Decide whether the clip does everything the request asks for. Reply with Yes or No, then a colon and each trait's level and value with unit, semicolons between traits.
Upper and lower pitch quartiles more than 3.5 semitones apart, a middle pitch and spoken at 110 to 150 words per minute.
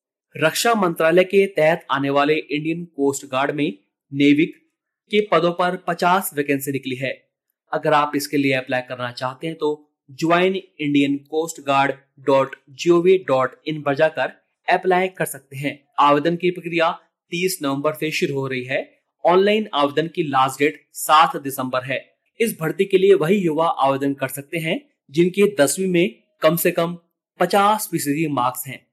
No: average, 4.2 semitones; medium, 155 Hz; average, 165 wpm